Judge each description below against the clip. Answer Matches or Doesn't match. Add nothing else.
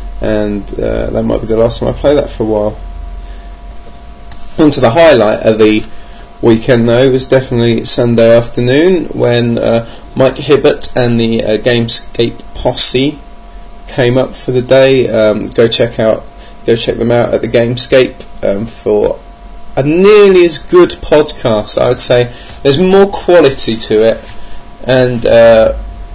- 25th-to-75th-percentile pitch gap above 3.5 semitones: Doesn't match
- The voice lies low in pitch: Matches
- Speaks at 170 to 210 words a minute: Doesn't match